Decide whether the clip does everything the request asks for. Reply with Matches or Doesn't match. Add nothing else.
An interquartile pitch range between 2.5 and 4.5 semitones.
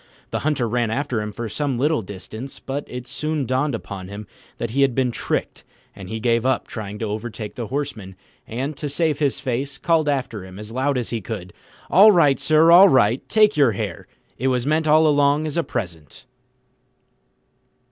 Doesn't match